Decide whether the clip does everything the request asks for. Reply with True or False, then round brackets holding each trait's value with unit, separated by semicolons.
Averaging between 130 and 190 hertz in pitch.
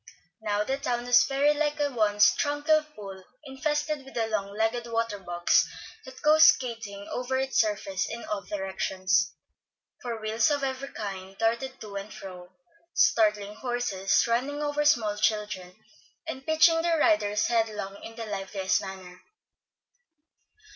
False (225 Hz)